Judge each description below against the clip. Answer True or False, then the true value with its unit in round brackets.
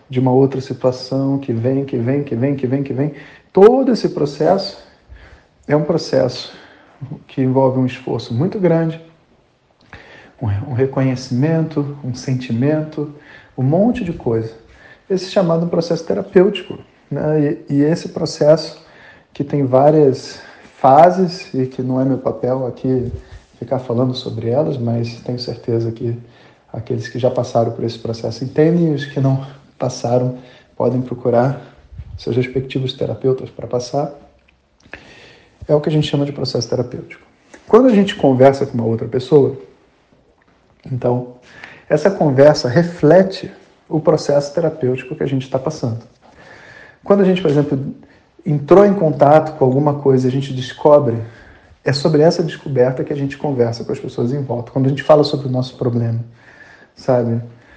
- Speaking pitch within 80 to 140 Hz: True (135 Hz)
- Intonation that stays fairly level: False (3.6 semitones)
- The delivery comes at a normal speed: True (150 wpm)